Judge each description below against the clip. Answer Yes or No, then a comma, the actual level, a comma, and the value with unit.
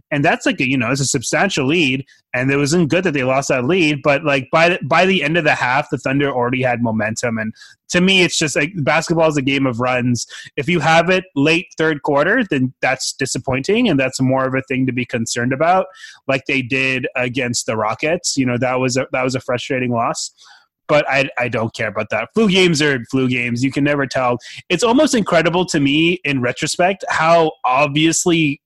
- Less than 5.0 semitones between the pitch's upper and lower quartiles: Yes, average, 4.0 semitones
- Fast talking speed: Yes, fast, 225 wpm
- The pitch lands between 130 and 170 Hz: Yes, medium, 140 Hz